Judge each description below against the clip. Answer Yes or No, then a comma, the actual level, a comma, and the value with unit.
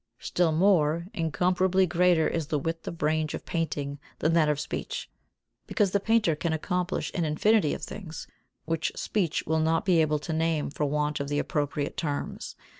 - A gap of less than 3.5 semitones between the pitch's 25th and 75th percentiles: Yes, average, 3.0 semitones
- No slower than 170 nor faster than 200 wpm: Yes, average, 180 wpm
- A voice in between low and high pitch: Yes, medium, 160 Hz